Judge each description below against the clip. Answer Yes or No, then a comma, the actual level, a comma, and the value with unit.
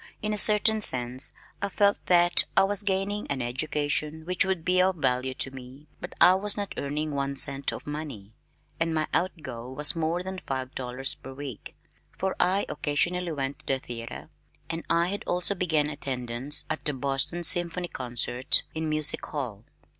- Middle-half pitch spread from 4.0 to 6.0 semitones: Yes, average, 5.2 semitones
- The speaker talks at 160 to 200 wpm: Yes, average, 180 wpm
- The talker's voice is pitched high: No, medium, 155 Hz